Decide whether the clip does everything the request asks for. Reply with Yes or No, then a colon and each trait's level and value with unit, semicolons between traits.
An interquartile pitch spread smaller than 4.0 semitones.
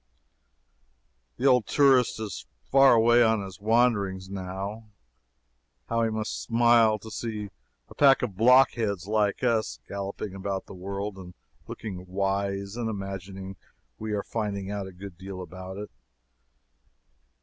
Yes: average, 2.8 semitones